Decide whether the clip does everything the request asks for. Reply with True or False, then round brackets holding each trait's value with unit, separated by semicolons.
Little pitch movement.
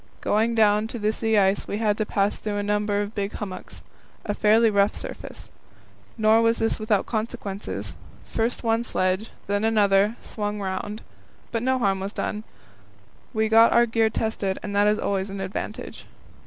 True (1.8 semitones)